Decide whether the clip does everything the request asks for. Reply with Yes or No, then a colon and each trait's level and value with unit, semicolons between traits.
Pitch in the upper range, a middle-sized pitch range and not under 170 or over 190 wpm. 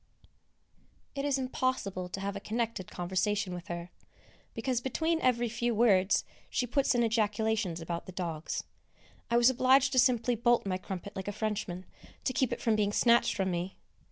Yes: high, 220 Hz; average, 4.5 semitones; average, 175 wpm